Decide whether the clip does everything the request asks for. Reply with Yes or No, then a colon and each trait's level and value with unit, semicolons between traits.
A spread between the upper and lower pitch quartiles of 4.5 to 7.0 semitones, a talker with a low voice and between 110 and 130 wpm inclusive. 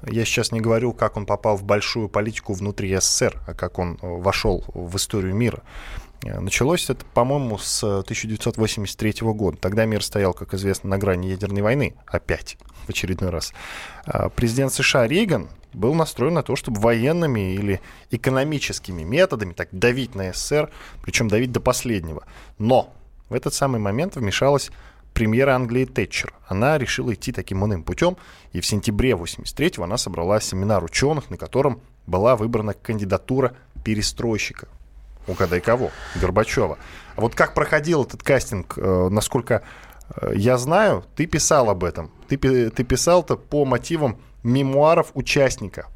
No: average, 4.9 semitones; low, 110 Hz; average, 145 wpm